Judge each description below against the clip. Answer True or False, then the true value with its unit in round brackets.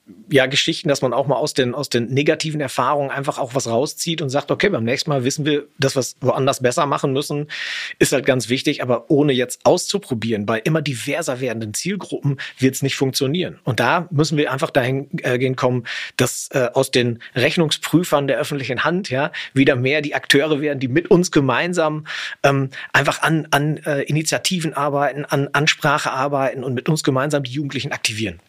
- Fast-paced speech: True (195 wpm)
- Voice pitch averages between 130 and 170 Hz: True (140 Hz)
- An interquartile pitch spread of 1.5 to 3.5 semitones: True (2.6 semitones)